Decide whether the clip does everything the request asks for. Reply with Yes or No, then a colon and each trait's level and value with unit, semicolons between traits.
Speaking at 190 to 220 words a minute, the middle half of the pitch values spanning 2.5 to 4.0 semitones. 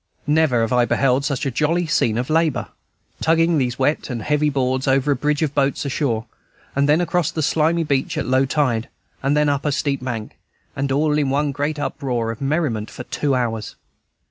Yes: average, 195 wpm; average, 2.9 semitones